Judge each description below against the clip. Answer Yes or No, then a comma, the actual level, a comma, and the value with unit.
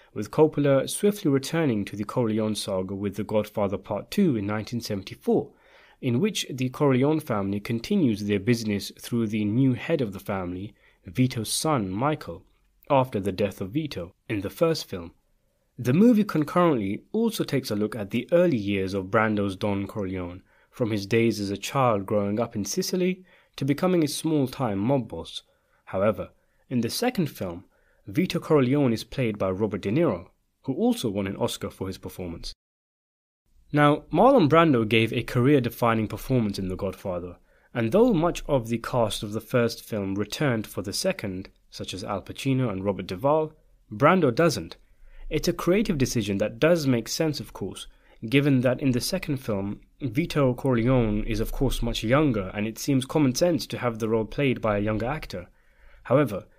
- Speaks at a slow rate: No, average, 175 wpm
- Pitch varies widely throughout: Yes, wide, 6.2 semitones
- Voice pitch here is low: Yes, low, 120 Hz